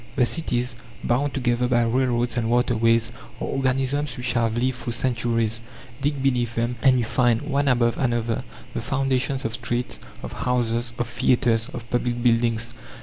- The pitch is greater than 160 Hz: No, low, 120 Hz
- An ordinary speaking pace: Yes, average, 160 wpm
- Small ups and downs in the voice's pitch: Yes, narrow, 1.6 semitones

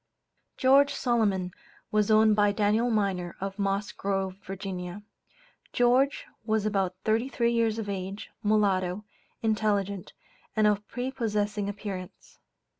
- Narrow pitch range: Yes, narrow, 2.2 semitones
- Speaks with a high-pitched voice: Yes, high, 210 Hz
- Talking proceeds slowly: Yes, slow, 115 wpm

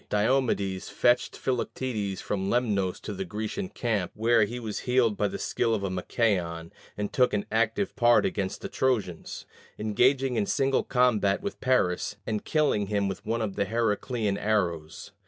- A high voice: No, low, 110 Hz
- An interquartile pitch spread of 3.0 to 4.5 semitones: Yes, average, 3.7 semitones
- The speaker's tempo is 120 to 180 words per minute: Yes, average, 160 wpm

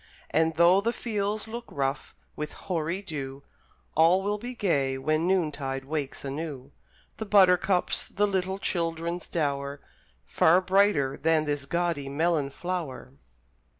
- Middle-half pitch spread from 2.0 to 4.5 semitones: No, average, 5.1 semitones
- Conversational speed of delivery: No, slow, 130 wpm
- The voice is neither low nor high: Yes, medium, 165 Hz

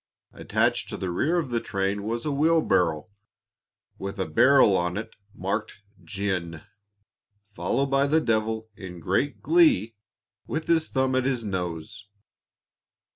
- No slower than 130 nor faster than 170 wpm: Yes, slow, 135 wpm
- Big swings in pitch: Yes, wide, 6.4 semitones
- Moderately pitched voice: No, low, 110 Hz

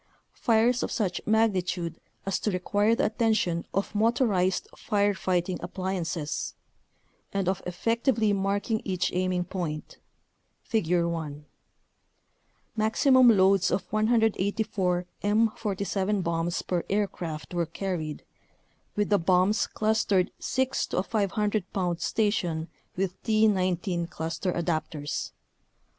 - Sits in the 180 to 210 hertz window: Yes, high, 190 Hz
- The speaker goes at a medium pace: No, slow, 110 wpm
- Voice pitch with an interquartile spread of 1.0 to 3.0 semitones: No, average, 3.5 semitones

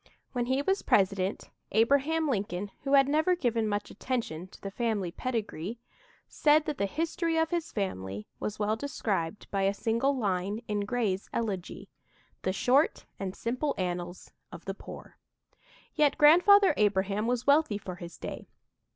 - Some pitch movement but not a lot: No, wide, 6.4 semitones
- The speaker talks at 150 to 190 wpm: Yes, average, 155 wpm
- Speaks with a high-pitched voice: Yes, high, 225 Hz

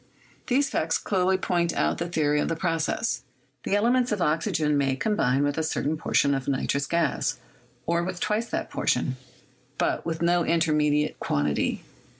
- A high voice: No, medium, 165 Hz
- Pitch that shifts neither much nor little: Yes, average, 3.8 semitones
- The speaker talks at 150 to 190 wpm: Yes, average, 160 wpm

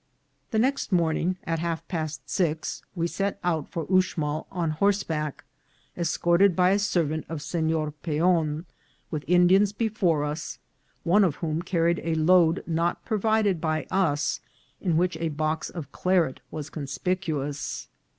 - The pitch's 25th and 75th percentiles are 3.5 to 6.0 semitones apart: No, average, 2.8 semitones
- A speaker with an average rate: Yes, average, 150 wpm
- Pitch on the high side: No, medium, 165 Hz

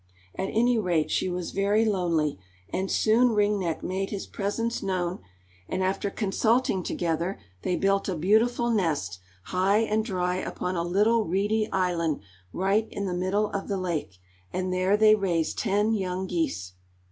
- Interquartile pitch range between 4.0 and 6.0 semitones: No, average, 2.9 semitones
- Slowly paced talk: No, average, 160 wpm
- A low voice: No, high, 190 Hz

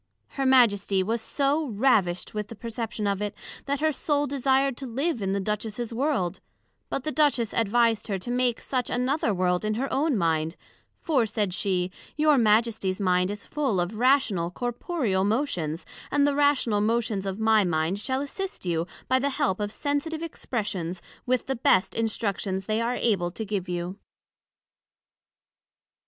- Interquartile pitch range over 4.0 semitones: Yes, wide, 5.6 semitones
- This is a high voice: Yes, high, 225 Hz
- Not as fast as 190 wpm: Yes, average, 165 wpm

